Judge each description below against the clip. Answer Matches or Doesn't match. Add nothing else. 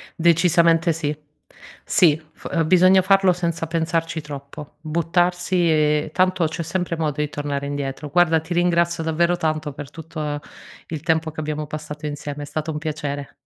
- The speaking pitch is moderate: Matches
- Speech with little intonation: Matches